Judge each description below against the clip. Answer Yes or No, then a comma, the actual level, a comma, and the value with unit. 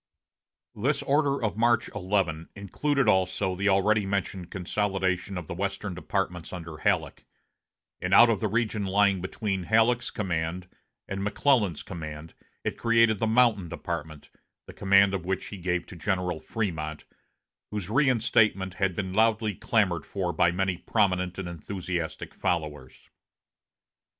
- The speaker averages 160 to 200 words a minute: No, average, 140 wpm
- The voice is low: Yes, very low, 95 Hz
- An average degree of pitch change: Yes, average, 3.3 semitones